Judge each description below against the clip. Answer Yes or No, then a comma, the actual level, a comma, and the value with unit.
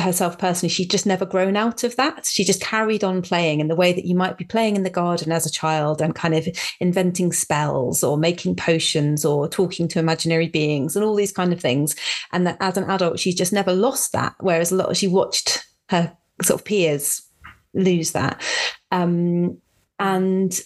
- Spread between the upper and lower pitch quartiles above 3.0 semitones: No, narrow, 2.6 semitones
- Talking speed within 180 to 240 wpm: Yes, fast, 205 wpm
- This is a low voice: No, medium, 180 Hz